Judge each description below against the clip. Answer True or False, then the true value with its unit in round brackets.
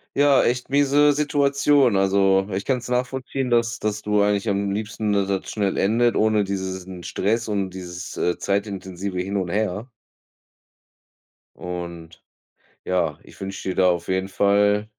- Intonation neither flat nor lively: True (3.7 semitones)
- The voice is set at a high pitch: False (100 Hz)